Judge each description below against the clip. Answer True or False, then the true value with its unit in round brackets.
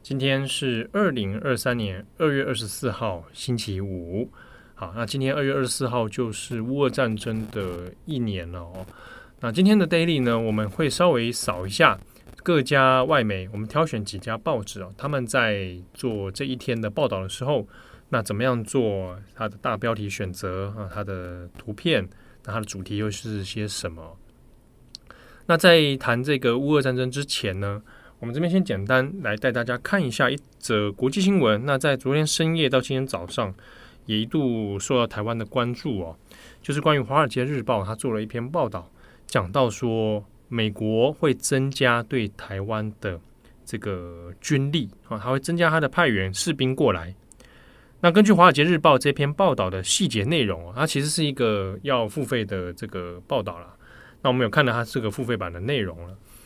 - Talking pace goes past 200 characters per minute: True (275 characters per minute)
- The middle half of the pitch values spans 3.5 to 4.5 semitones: False (4.9 semitones)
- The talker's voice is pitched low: True (120 Hz)